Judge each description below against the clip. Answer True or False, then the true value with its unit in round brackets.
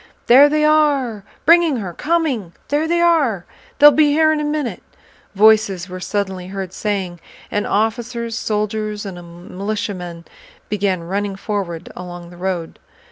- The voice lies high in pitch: True (210 Hz)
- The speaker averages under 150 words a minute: True (140 wpm)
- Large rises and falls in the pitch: True (7.7 semitones)